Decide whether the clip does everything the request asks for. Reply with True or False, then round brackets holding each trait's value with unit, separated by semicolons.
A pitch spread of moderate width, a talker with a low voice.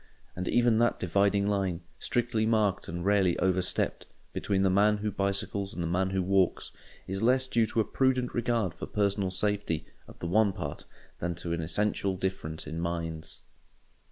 True (3.1 semitones; 100 Hz)